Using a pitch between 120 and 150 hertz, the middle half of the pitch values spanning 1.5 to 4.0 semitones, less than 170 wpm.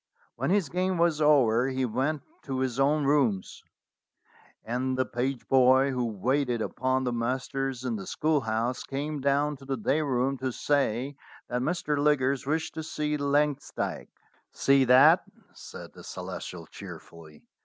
Yes: low, 135 Hz; average, 2.8 semitones; average, 150 wpm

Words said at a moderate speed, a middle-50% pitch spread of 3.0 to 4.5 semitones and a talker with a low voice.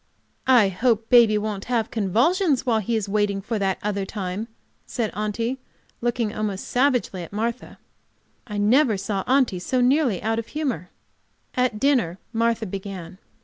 No: average, 150 wpm; average, 3.6 semitones; high, 220 Hz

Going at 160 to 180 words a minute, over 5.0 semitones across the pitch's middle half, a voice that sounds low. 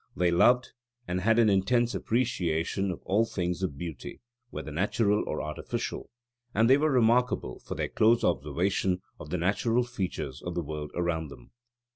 Yes: average, 165 wpm; wide, 5.4 semitones; very low, 95 Hz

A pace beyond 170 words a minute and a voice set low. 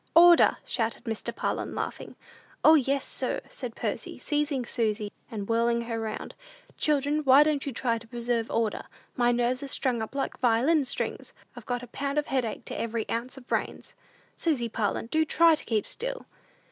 No: average, 180 wpm; high, 245 Hz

